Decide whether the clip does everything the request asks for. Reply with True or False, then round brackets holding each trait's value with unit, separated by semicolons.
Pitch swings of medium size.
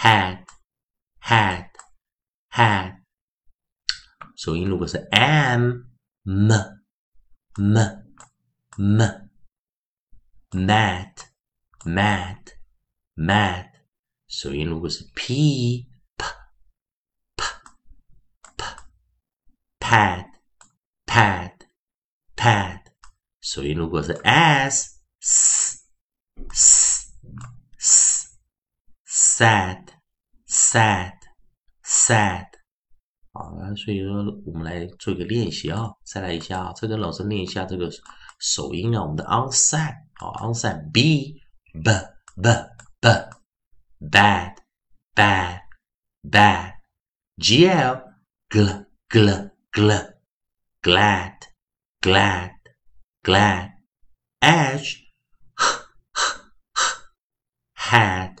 True (4.4 semitones)